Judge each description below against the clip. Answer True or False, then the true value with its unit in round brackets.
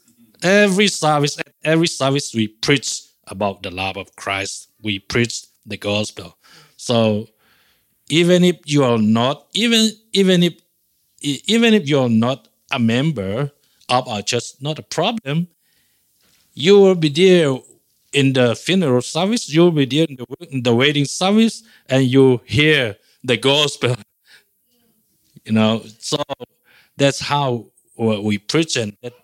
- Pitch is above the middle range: False (140 Hz)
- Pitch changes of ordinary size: False (6.2 semitones)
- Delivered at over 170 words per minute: False (135 wpm)